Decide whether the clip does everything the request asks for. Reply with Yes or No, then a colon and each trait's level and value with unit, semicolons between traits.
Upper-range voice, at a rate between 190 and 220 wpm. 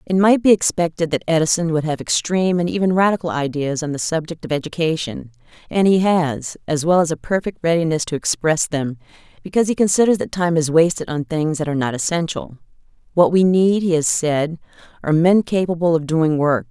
No: medium, 165 Hz; average, 195 wpm